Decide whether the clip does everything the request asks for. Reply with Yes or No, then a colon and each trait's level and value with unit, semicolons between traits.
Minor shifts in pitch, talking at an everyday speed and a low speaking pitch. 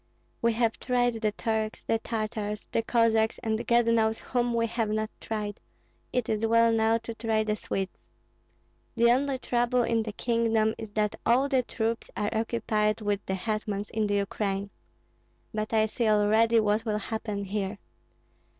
No: narrow, 1.5 semitones; average, 170 wpm; high, 220 Hz